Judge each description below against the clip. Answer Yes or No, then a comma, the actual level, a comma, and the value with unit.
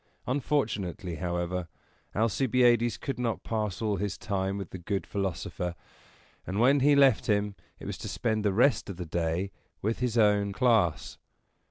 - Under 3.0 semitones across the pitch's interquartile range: No, average, 4.3 semitones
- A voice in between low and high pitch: No, low, 105 Hz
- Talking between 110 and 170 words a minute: Yes, average, 160 wpm